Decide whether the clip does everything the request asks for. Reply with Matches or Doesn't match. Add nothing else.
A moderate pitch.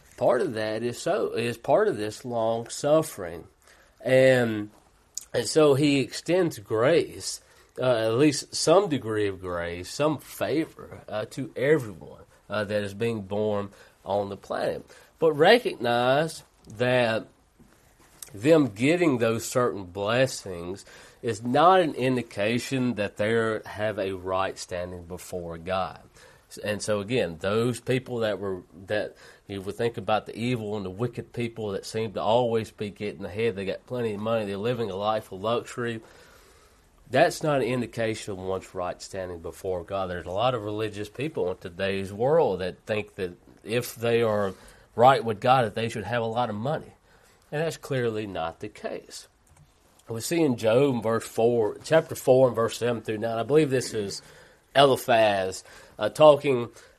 Doesn't match